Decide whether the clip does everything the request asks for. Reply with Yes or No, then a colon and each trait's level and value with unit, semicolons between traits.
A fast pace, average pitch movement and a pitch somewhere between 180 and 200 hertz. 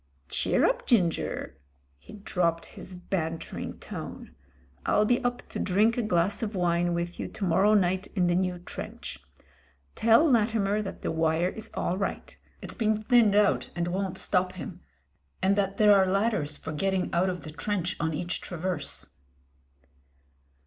No: average, 170 wpm; average, 3.2 semitones; high, 190 Hz